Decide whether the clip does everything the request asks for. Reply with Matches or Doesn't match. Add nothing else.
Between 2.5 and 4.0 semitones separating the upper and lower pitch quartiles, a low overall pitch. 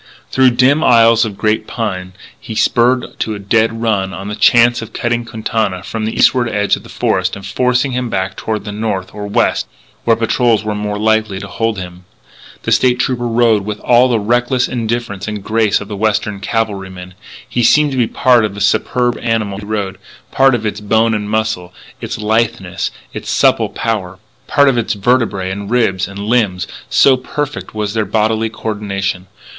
Matches